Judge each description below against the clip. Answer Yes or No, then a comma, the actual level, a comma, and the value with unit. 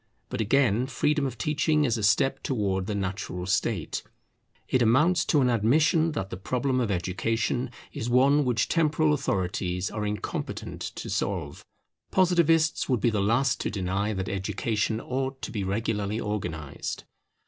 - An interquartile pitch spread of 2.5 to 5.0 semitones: No, wide, 5.6 semitones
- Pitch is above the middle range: No, low, 115 Hz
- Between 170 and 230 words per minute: No, average, 155 wpm